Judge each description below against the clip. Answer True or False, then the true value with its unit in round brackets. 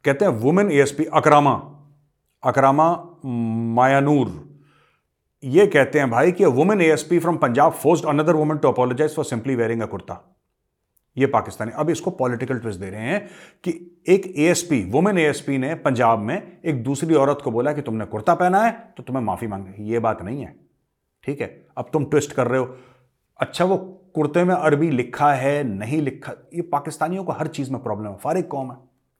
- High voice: False (140 Hz)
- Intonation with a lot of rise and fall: False (4.5 semitones)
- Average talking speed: False (195 wpm)